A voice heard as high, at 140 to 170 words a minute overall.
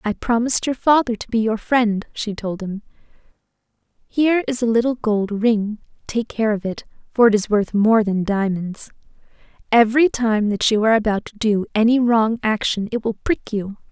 No: high, 220 Hz; average, 185 wpm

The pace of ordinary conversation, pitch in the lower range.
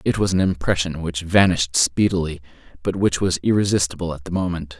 Yes: average, 175 wpm; very low, 85 Hz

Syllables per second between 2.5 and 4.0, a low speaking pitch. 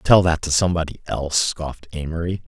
No: 6.1 syllables/s; very low, 80 Hz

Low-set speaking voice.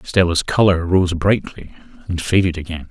Yes: very low, 90 Hz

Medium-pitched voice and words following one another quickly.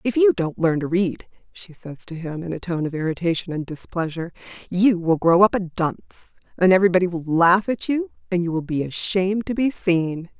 Yes: medium, 180 Hz; fast, 220 wpm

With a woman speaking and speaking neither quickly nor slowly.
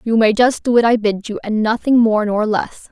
No: female; fast, 270 wpm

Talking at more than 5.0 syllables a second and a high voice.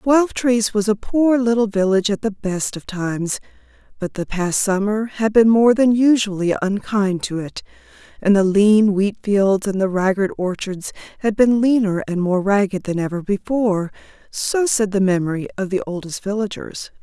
No: 4.8 syllables/s; high, 205 Hz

